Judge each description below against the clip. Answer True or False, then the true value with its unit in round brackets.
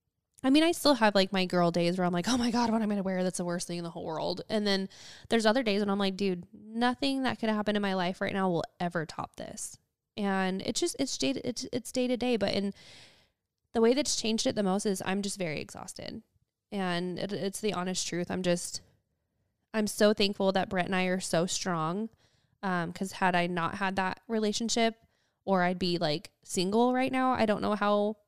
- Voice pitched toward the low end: False (195 Hz)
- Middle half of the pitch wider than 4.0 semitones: False (3.7 semitones)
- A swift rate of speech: True (240 wpm)